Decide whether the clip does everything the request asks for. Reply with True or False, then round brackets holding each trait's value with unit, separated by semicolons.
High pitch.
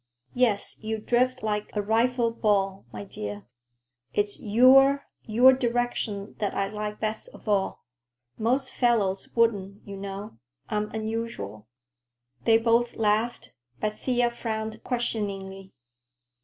True (220 Hz)